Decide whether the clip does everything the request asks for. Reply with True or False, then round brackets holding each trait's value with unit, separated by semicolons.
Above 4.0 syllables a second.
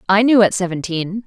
True (5.5 syllables/s)